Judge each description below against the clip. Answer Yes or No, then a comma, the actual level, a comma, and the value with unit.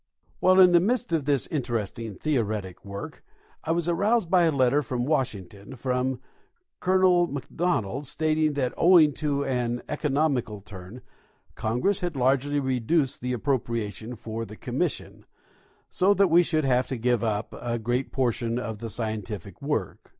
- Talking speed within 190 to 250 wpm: No, average, 150 wpm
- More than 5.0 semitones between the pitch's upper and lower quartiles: Yes, wide, 5.5 semitones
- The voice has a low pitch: Yes, low, 130 Hz